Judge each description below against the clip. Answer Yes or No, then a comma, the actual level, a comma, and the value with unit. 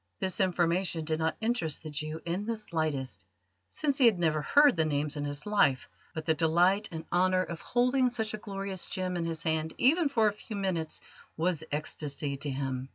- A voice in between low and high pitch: Yes, medium, 170 Hz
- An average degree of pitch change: Yes, average, 5.0 semitones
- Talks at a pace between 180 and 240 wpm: Yes, average, 200 wpm